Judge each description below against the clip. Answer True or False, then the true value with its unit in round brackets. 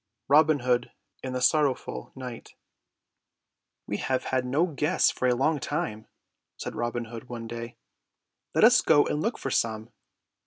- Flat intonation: False (3.5 semitones)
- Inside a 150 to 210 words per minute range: True (160 wpm)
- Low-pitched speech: True (125 Hz)